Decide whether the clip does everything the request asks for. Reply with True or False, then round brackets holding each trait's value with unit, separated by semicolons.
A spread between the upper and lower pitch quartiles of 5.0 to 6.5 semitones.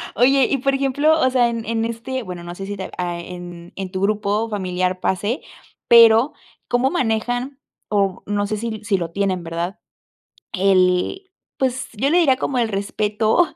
True (5.3 semitones)